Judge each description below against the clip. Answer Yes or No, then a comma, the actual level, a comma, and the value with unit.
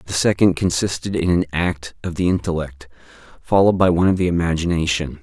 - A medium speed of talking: Yes, average, 170 wpm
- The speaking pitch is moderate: No, very low, 85 Hz